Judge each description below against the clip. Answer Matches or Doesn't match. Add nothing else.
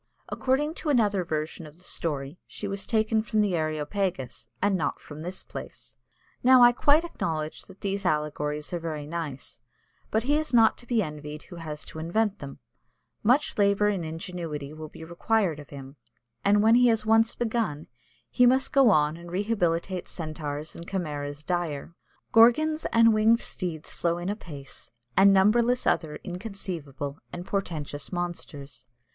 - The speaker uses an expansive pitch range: Matches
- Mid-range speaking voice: Matches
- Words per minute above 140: Matches